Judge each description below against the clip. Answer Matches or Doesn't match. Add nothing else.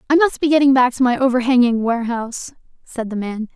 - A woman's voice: Matches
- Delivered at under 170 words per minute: Doesn't match